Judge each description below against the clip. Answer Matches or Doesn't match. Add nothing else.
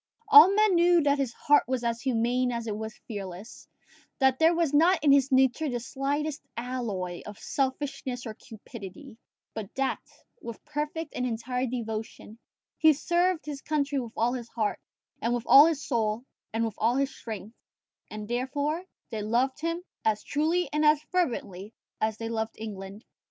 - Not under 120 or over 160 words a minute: Doesn't match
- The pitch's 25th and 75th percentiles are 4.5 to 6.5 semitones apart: Matches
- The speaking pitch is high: Matches